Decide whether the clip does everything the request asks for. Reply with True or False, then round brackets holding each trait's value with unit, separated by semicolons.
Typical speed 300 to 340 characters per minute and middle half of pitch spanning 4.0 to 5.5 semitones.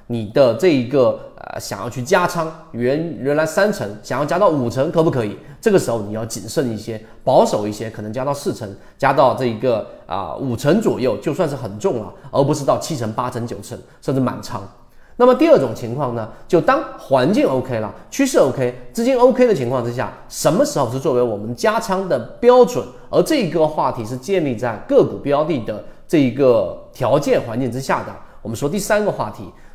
False (305 characters per minute; 6.5 semitones)